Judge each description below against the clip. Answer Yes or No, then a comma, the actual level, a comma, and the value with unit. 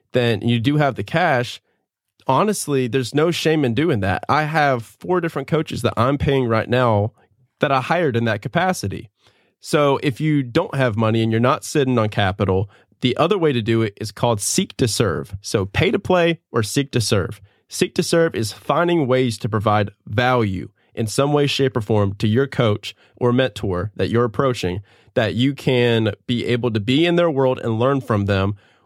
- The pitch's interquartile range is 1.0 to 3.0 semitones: No, average, 4.3 semitones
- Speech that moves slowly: No, average, 200 wpm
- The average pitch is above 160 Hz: No, low, 125 Hz